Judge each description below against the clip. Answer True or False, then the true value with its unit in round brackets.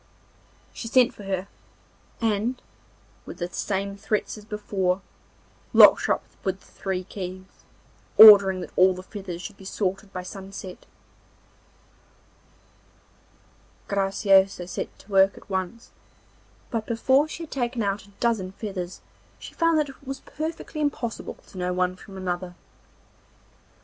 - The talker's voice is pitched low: False (195 Hz)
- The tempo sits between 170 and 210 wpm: False (140 wpm)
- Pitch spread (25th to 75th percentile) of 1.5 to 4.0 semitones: True (3.3 semitones)